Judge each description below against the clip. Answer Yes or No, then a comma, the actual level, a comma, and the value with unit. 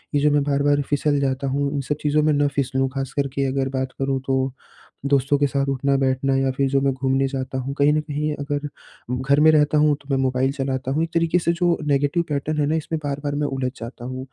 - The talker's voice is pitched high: No, medium, 140 Hz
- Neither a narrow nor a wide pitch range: No, narrow, 1.6 semitones